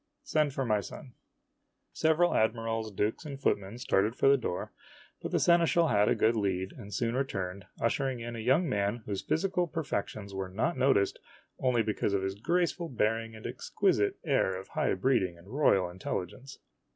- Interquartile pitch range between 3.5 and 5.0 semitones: No, wide, 5.6 semitones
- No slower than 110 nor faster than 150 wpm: No, average, 175 wpm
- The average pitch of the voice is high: No, low, 115 Hz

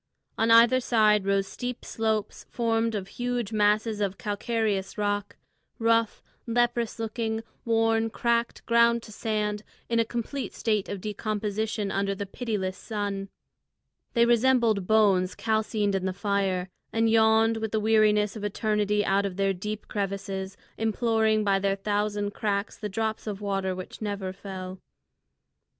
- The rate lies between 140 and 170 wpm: Yes, average, 145 wpm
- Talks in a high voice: Yes, high, 210 Hz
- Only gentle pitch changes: Yes, narrow, 2.2 semitones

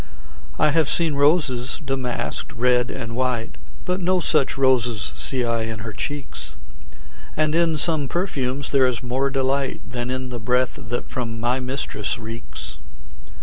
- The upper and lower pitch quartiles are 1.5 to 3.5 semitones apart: Yes, average, 2.9 semitones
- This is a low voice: Yes, low, 130 Hz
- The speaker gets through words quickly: No, average, 150 wpm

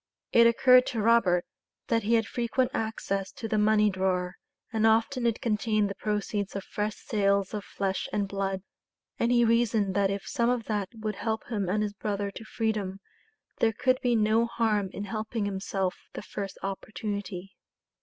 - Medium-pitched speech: No, high, 210 Hz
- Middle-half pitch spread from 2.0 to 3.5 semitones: Yes, narrow, 2.4 semitones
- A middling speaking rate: Yes, average, 175 wpm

